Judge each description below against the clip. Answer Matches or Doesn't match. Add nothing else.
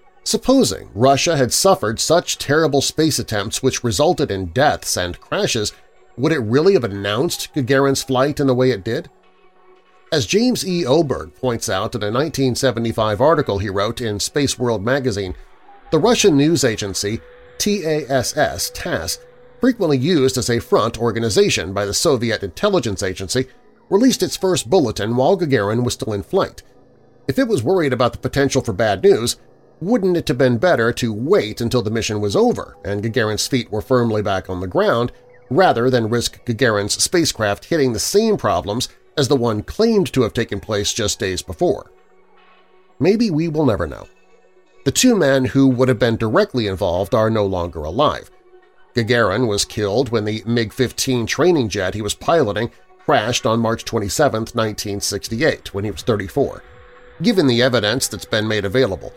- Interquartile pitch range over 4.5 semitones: Matches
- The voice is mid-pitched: Doesn't match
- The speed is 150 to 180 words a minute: Matches